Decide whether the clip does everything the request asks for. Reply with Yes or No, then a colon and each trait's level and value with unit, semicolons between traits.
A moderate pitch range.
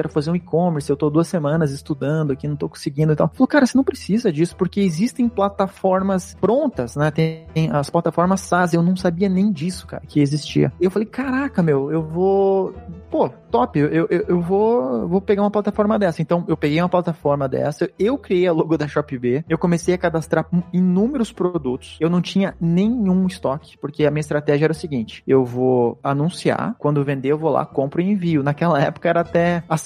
Yes: average, 4.3 semitones